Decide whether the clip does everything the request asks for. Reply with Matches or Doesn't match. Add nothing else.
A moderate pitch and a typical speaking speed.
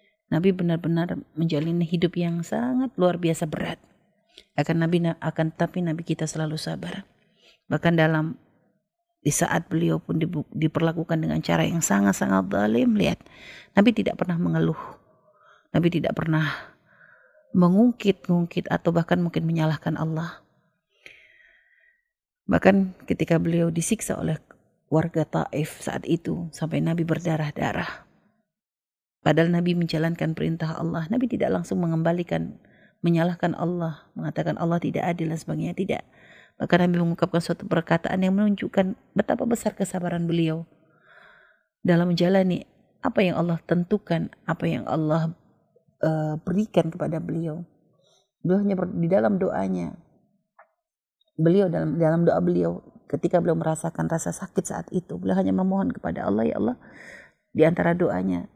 Matches